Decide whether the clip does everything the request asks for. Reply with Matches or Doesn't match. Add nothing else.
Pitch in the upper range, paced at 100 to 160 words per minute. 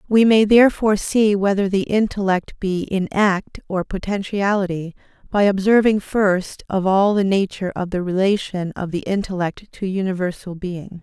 Matches